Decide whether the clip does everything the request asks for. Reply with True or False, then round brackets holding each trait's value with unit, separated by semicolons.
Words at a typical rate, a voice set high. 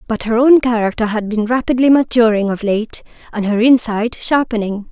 True (170 wpm; 230 Hz)